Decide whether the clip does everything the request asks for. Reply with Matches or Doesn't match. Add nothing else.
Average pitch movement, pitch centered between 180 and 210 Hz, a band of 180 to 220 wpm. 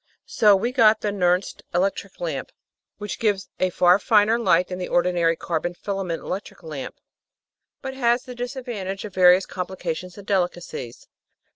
Doesn't match